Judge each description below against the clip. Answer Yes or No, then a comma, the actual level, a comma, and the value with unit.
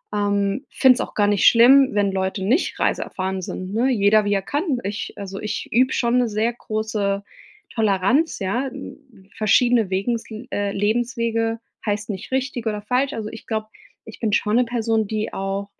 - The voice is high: Yes, high, 220 Hz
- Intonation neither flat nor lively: Yes, average, 3.1 semitones